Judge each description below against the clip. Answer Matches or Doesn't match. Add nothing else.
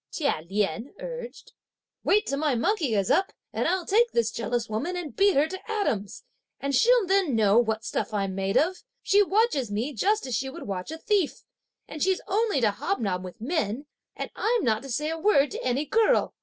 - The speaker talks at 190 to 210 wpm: Matches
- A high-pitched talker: Matches